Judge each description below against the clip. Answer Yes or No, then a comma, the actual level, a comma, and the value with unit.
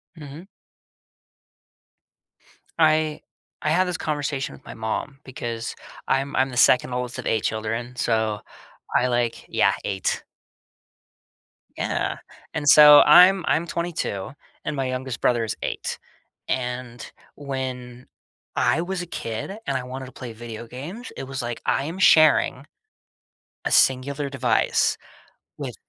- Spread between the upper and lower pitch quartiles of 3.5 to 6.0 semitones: Yes, average, 3.8 semitones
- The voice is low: Yes, low, 130 Hz